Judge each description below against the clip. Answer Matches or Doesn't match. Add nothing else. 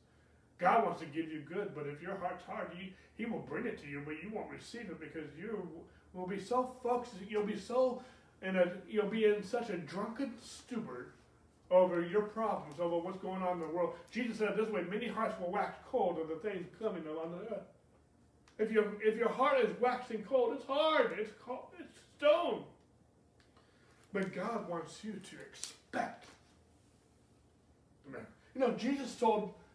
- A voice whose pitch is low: Doesn't match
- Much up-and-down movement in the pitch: Doesn't match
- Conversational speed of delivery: Matches